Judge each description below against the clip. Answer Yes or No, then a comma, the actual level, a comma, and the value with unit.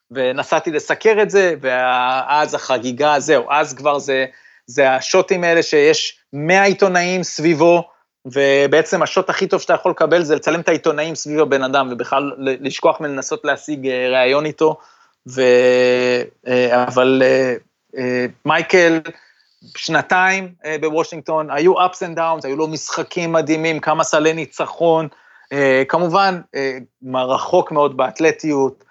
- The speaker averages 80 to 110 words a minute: No, average, 120 wpm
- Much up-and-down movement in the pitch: No, average, 4.3 semitones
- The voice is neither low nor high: Yes, medium, 155 Hz